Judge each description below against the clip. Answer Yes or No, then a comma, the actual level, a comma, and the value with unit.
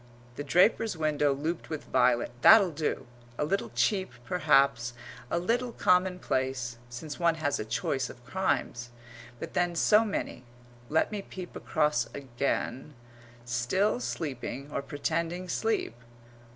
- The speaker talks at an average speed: No, slow, 130 wpm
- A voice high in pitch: No, medium, 150 Hz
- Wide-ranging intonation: Yes, wide, 5.8 semitones